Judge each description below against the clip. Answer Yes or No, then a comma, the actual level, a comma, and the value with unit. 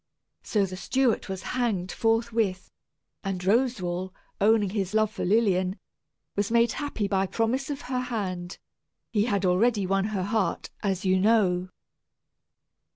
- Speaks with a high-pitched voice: Yes, high, 205 Hz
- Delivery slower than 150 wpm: Yes, average, 140 wpm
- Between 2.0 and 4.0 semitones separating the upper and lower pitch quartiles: Yes, average, 3.5 semitones